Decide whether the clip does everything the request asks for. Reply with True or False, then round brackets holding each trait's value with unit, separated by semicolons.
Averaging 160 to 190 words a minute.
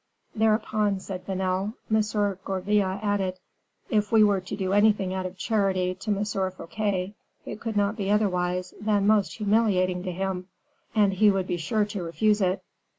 True (165 wpm)